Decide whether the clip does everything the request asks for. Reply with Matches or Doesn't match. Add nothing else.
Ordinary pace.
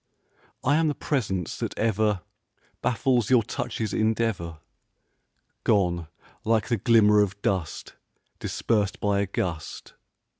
Doesn't match